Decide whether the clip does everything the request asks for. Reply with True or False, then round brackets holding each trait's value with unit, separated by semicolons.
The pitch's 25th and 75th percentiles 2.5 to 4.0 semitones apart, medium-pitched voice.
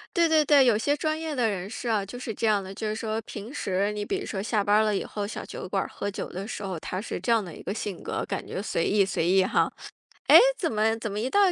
False (3.2 semitones; 215 Hz)